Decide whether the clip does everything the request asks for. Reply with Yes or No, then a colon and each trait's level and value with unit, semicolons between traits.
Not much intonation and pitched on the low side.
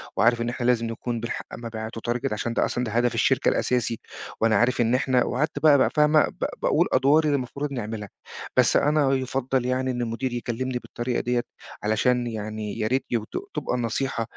Yes: narrow, 2.2 semitones; low, 120 Hz